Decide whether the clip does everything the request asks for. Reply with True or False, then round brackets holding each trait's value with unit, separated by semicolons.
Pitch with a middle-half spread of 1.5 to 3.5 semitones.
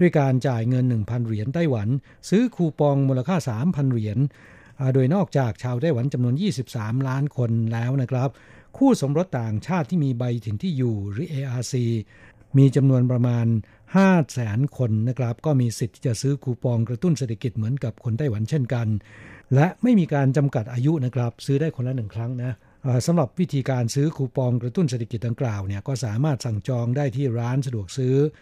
True (3.2 semitones)